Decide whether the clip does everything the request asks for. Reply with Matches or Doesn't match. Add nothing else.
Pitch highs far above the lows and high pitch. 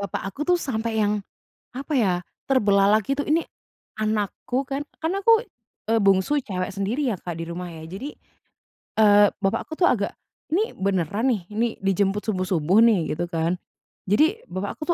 Matches